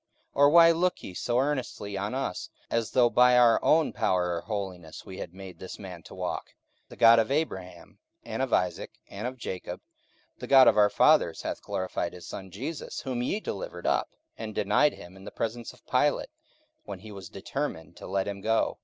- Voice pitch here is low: Yes, low, 105 Hz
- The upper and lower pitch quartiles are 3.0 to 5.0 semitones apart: No, wide, 5.6 semitones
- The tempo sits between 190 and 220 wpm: Yes, fast, 205 wpm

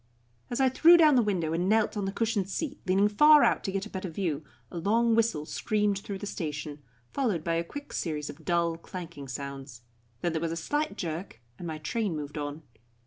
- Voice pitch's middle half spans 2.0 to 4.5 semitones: No, wide, 5.6 semitones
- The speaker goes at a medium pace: No, fast, 215 wpm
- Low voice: No, medium, 185 Hz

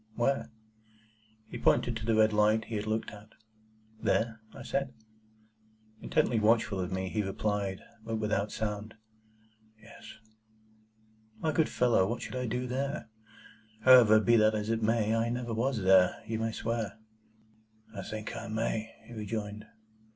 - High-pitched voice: No, low, 110 Hz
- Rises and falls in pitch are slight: Yes, narrow, 1.8 semitones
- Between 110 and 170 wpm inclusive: Yes, average, 150 wpm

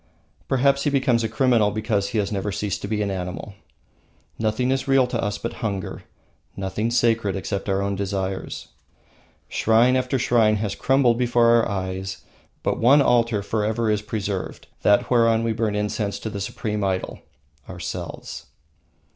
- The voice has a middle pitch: No, low, 110 Hz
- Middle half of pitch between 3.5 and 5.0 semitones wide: No, average, 2.8 semitones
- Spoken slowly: No, average, 160 wpm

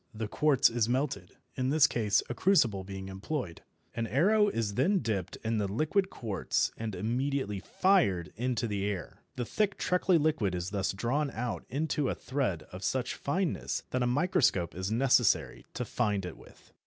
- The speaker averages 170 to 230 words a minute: Yes, average, 175 wpm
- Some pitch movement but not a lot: No, wide, 6.5 semitones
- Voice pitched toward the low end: Yes, low, 120 Hz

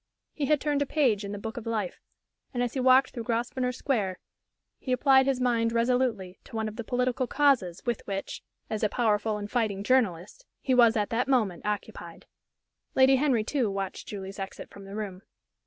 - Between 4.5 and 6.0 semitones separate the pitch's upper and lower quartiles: No, average, 3.9 semitones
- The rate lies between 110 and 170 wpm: No, average, 195 wpm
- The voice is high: Yes, high, 230 Hz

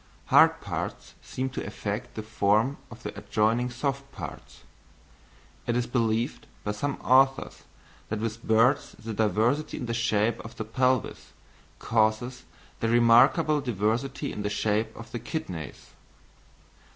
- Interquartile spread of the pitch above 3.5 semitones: No, average, 2.9 semitones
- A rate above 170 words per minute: No, slow, 135 wpm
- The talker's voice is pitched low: Yes, low, 115 Hz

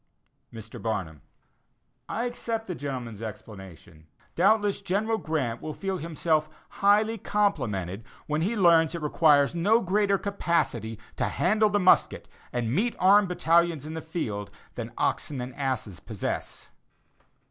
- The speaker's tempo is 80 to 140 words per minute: Yes, slow, 135 wpm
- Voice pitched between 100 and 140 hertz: No, medium, 160 Hz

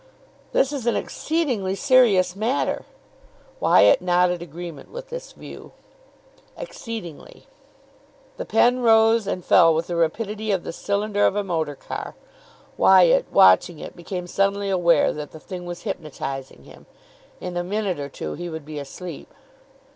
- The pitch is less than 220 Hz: Yes, medium, 185 Hz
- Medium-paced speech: Yes, average, 145 wpm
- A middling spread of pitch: Yes, average, 4.5 semitones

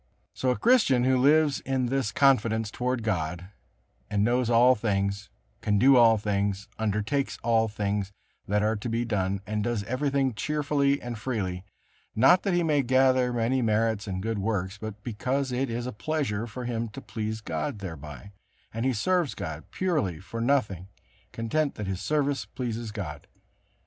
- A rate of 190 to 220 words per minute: No, average, 170 wpm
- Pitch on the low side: Yes, low, 115 Hz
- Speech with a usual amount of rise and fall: Yes, average, 4.2 semitones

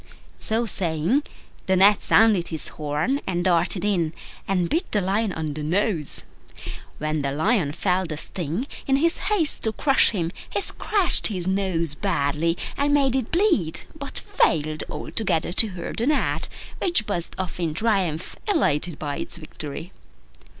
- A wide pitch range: Yes, wide, 5.8 semitones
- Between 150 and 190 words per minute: Yes, average, 155 wpm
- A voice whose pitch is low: No, medium, 185 Hz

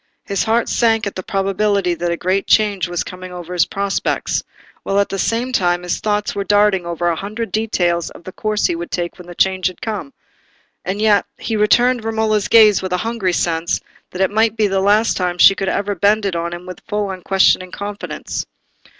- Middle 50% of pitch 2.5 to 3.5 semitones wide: Yes, average, 2.9 semitones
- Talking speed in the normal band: No, fast, 210 wpm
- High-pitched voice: Yes, high, 195 Hz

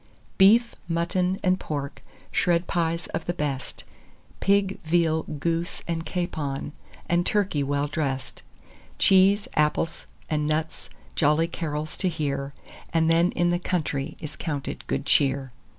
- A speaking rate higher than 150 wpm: No, slow, 135 wpm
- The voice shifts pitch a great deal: No, average, 2.9 semitones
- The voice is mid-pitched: Yes, medium, 165 Hz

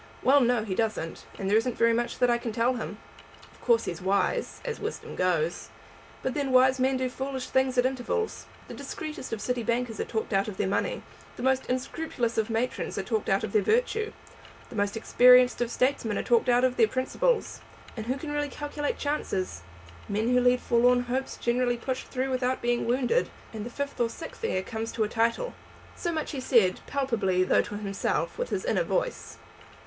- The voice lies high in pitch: Yes, high, 245 Hz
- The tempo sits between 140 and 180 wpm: No, fast, 205 wpm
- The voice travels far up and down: No, average, 3.0 semitones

